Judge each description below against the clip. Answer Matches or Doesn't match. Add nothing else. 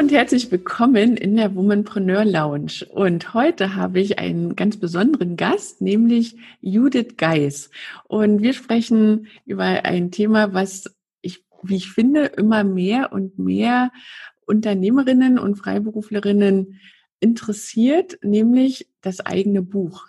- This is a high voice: Matches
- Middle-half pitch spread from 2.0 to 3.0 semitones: Doesn't match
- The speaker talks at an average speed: Doesn't match